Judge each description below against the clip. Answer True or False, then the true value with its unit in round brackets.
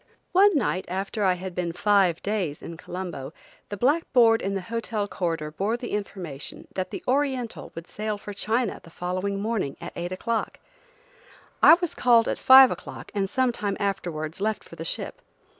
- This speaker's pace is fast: False (175 wpm)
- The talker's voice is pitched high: True (200 Hz)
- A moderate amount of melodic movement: True (4.4 semitones)